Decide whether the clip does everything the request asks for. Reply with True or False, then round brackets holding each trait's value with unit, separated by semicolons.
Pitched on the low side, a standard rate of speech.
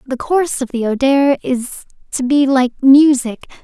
False (265 Hz; 165 wpm)